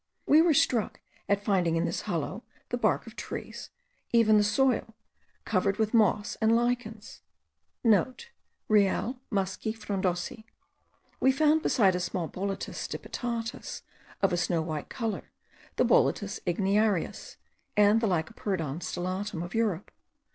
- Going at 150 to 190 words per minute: No, average, 140 wpm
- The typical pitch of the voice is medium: No, high, 205 Hz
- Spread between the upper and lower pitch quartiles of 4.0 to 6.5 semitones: No, average, 3.6 semitones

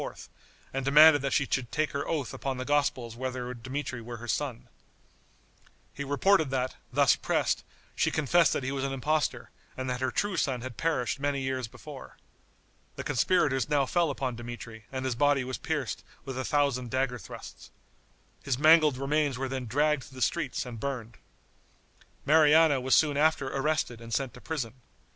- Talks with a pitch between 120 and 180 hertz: Yes, low, 135 Hz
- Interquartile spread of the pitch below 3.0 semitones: Yes, narrow, 2.6 semitones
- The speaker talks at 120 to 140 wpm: No, average, 175 wpm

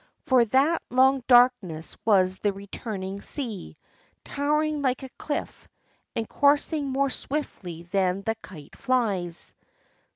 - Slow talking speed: Yes, slow, 120 wpm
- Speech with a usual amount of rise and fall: No, wide, 6.3 semitones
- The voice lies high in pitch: Yes, high, 240 Hz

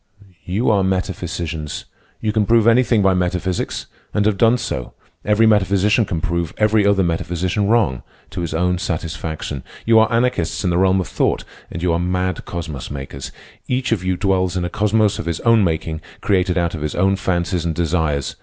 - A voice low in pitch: Yes, very low, 90 Hz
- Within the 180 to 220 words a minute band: Yes, average, 185 wpm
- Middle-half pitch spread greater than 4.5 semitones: No, average, 3.6 semitones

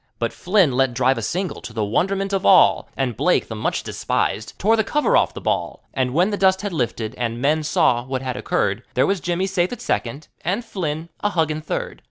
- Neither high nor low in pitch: Yes, medium, 160 Hz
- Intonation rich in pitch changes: Yes, wide, 7.5 semitones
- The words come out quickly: Yes, fast, 225 wpm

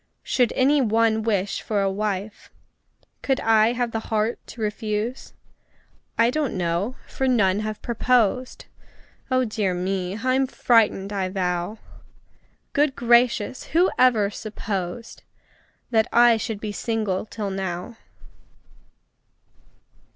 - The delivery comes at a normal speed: No, slow, 120 wpm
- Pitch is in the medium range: No, high, 220 Hz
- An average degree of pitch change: Yes, average, 3.4 semitones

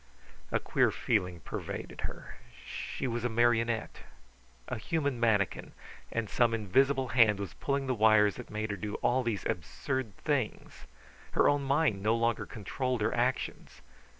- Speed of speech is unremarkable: Yes, average, 150 wpm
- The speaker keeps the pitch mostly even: No, average, 3.6 semitones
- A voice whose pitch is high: No, low, 115 Hz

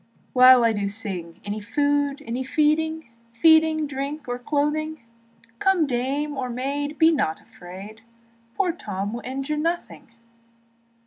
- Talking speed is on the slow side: Yes, slow, 130 wpm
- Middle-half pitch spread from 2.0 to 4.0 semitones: No, average, 4.8 semitones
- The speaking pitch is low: No, very high, 275 Hz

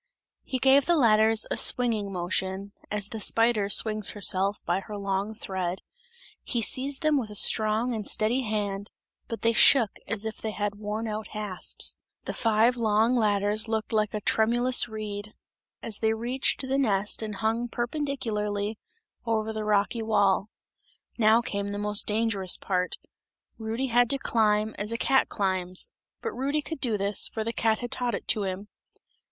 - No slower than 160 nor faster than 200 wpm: Yes, average, 170 wpm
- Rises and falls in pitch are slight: Yes, narrow, 2.3 semitones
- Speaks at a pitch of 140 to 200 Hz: No, high, 215 Hz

